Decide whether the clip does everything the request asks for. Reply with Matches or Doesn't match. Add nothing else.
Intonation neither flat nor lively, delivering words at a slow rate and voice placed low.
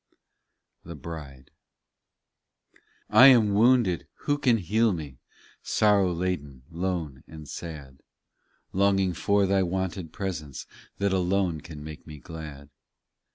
Matches